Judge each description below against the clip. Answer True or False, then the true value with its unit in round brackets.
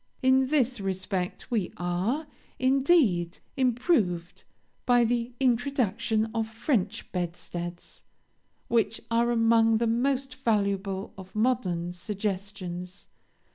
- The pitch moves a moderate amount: True (4.7 semitones)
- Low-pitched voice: False (225 Hz)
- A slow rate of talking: True (95 wpm)